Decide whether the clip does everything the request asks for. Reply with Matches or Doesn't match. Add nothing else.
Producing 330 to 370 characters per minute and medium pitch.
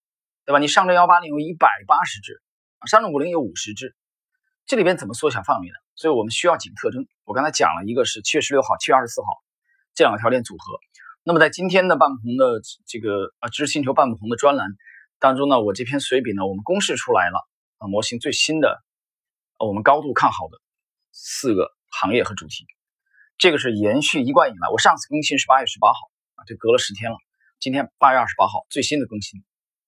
Matches